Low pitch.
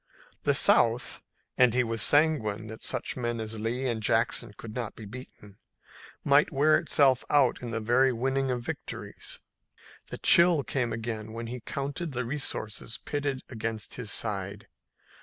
Yes: low, 120 Hz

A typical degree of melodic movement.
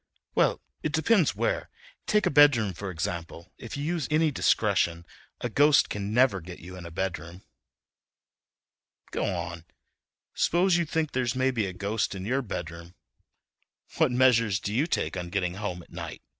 No: wide, 7.9 semitones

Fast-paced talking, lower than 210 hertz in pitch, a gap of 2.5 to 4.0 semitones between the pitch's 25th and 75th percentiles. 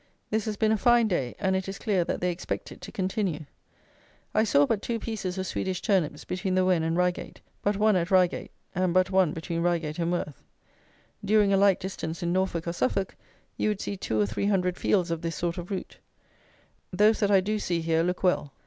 Yes: fast, 220 wpm; medium, 185 Hz; average, 2.8 semitones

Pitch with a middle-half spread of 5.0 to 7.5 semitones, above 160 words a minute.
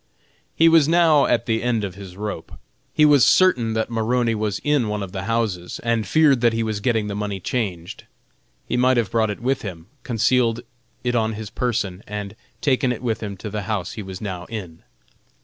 No: average, 3.3 semitones; average, 200 wpm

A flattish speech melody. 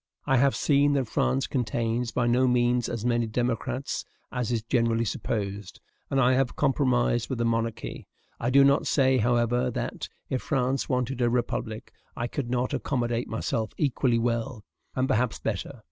Yes: narrow, 1.9 semitones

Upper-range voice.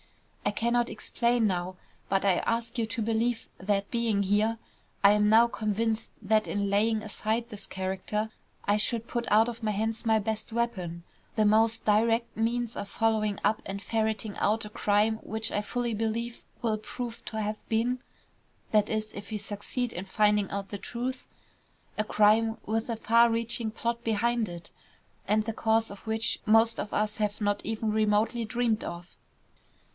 Yes: high, 220 Hz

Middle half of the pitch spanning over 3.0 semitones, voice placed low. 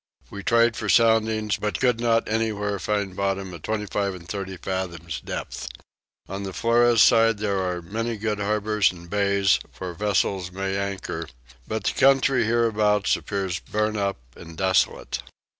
No: narrow, 2.5 semitones; low, 100 Hz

